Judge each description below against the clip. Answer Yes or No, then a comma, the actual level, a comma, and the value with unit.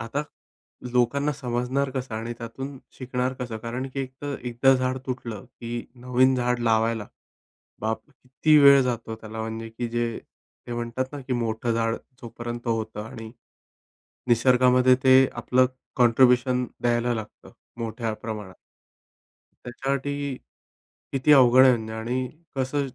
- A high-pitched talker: No, low, 125 Hz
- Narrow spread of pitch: Yes, narrow, 2.2 semitones